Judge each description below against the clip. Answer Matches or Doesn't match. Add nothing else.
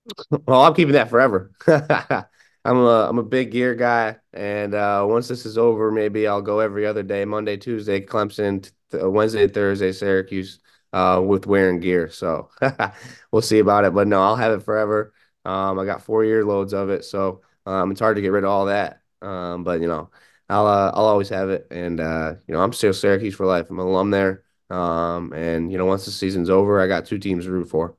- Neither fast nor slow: Doesn't match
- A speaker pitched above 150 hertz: Doesn't match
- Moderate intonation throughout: Doesn't match